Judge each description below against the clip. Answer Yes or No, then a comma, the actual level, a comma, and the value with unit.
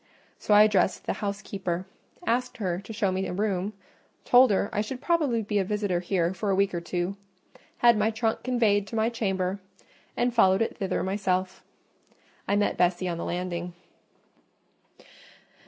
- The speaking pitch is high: Yes, high, 200 Hz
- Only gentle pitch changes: No, average, 3.1 semitones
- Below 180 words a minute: Yes, average, 170 wpm